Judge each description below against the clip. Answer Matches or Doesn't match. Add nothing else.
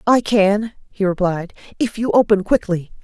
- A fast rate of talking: Doesn't match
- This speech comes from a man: Doesn't match